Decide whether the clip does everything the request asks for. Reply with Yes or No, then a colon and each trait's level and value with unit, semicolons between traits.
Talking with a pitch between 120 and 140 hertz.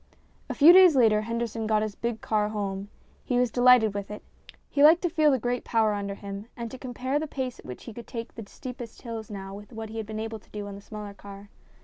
No: high, 225 Hz